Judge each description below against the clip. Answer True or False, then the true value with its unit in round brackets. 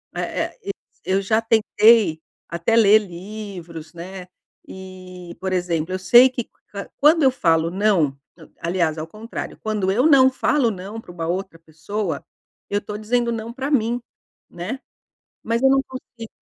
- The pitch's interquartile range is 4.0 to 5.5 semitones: True (4.7 semitones)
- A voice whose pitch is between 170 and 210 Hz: True (205 Hz)